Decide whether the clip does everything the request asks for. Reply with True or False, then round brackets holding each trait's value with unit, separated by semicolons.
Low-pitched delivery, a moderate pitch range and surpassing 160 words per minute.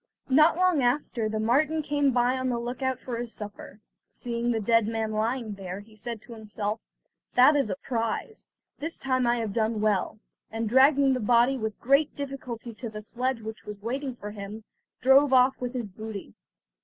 False (235 Hz; 3.3 semitones; 190 wpm)